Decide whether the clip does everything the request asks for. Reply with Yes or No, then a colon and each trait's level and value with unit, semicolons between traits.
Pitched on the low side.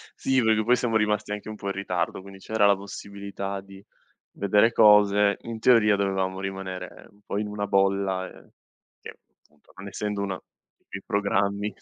Yes: low, 100 Hz